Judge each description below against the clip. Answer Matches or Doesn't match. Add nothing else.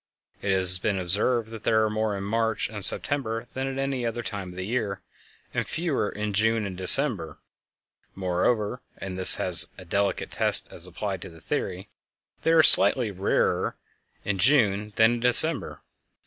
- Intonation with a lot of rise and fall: Doesn't match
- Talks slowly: Doesn't match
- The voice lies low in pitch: Matches